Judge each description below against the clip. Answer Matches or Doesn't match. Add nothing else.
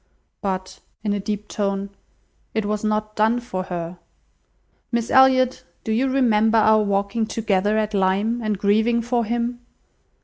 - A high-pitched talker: Matches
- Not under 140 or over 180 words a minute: Matches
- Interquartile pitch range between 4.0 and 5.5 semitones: Doesn't match